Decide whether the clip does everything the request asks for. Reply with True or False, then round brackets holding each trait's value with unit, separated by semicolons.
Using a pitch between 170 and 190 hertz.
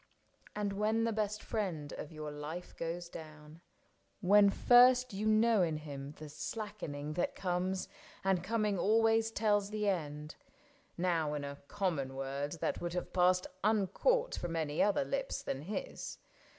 True (185 Hz)